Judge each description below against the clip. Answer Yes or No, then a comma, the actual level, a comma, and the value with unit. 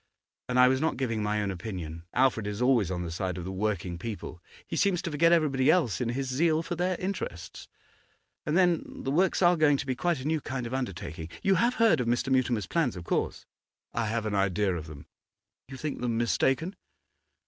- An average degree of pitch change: No, wide, 7.4 semitones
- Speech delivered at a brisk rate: Yes, fast, 215 wpm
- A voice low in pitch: Yes, low, 125 Hz